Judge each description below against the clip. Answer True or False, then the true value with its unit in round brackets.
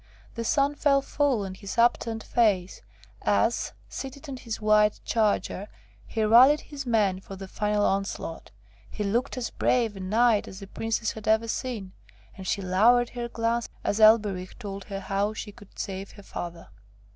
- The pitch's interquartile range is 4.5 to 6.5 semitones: False (3.3 semitones)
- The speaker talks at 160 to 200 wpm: True (170 wpm)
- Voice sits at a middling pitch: False (215 Hz)